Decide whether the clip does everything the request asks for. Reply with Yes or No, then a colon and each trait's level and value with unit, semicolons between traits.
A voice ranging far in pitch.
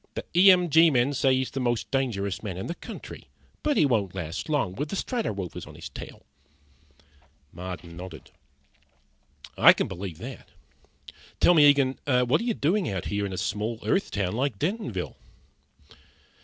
Yes: wide, 7.8 semitones